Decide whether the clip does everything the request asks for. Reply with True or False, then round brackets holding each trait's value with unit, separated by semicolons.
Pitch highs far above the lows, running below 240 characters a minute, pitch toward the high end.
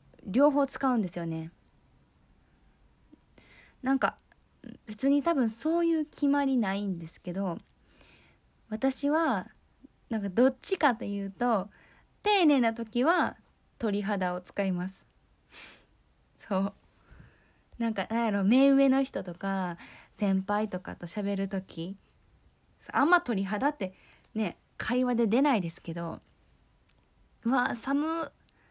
True (6.0 semitones; 205 characters per minute; 220 Hz)